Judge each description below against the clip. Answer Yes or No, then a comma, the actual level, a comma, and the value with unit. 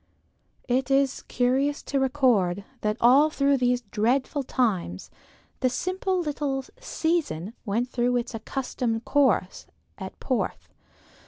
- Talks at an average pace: No, slow, 115 wpm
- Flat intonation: No, average, 3.4 semitones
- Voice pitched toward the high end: Yes, very high, 255 Hz